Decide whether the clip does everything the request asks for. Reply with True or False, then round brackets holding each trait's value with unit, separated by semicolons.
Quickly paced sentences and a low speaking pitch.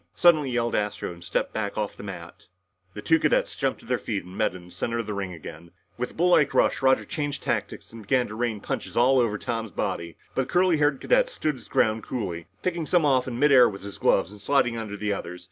True (250 wpm; 115 Hz)